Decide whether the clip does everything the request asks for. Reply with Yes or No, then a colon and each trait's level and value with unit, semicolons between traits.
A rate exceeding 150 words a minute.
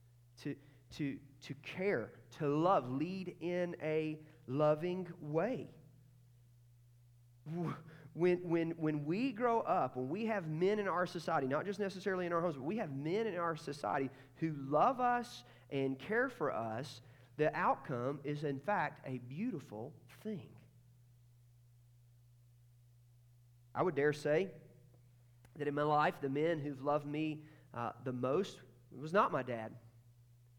No: average, 145 wpm